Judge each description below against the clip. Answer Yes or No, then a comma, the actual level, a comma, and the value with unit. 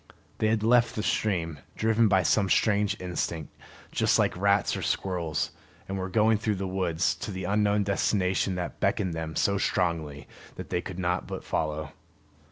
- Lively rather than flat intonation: No, average, 3.6 semitones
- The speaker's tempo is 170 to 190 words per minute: Yes, average, 175 wpm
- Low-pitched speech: Yes, very low, 95 Hz